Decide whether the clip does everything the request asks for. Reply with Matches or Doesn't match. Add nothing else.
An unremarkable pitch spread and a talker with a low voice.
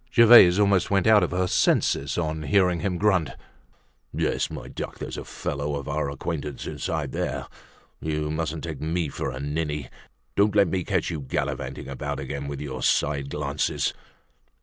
Matches